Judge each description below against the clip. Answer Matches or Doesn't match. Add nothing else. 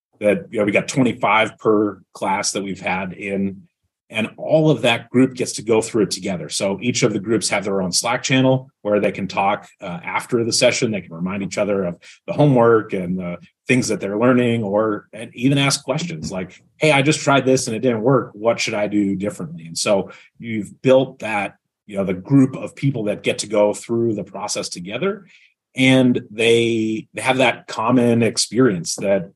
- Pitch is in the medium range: Doesn't match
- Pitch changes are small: Doesn't match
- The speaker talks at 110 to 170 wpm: Doesn't match